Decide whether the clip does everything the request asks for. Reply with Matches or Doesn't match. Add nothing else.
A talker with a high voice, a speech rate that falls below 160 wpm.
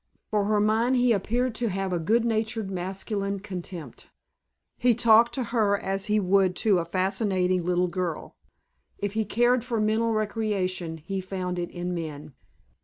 Doesn't match